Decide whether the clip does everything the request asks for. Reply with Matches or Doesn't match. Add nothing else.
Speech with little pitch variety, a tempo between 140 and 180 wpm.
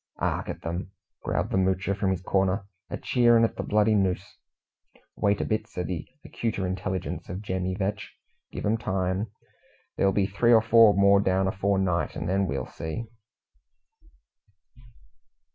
Matches